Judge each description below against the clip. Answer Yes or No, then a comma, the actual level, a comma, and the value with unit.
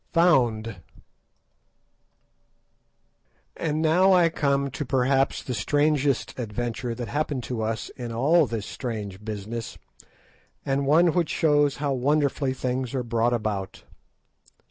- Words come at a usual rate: No, slow, 120 wpm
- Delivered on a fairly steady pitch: No, average, 4.2 semitones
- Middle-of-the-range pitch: No, low, 130 Hz